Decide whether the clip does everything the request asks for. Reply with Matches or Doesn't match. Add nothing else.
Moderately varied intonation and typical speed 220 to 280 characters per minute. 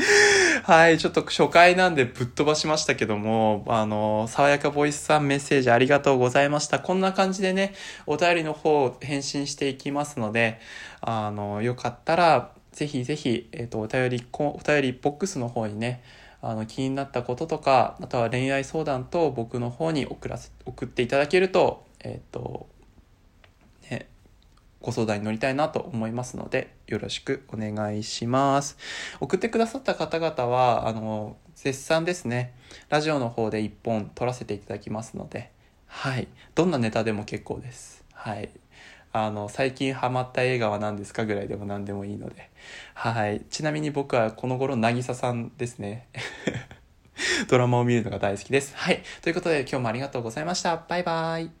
Doesn't match